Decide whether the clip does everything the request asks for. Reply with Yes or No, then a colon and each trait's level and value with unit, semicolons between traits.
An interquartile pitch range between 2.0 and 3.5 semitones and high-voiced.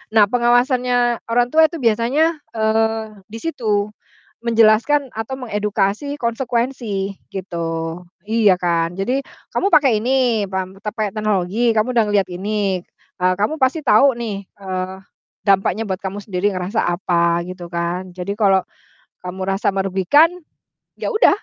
No: average, 4.1 semitones; high, 210 Hz